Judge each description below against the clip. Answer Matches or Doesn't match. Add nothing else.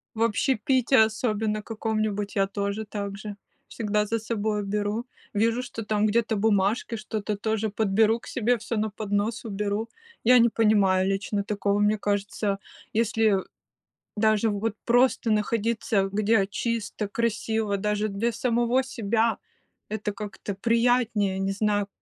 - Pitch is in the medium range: Doesn't match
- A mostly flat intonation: Matches